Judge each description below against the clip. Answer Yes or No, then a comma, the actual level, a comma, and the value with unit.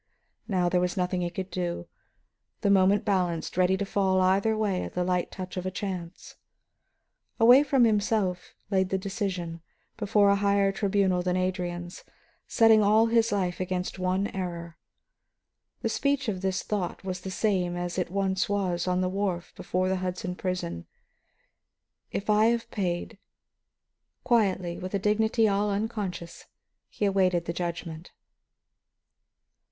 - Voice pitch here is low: No, high, 190 Hz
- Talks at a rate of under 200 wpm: Yes, average, 150 wpm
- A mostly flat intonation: Yes, narrow, 2.1 semitones